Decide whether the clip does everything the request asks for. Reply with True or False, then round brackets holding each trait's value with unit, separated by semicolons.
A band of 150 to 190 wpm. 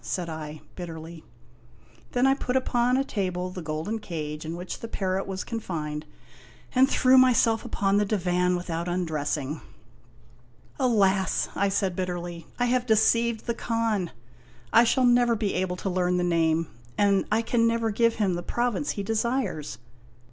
True (170 wpm)